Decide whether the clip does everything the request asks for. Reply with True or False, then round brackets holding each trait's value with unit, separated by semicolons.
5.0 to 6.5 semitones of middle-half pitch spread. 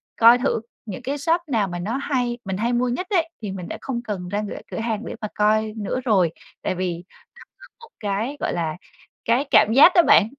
False (4.3 semitones)